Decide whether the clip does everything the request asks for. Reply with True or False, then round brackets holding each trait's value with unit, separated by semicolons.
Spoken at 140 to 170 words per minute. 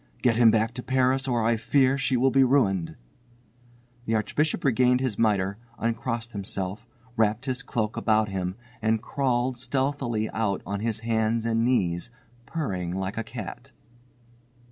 True (150 wpm)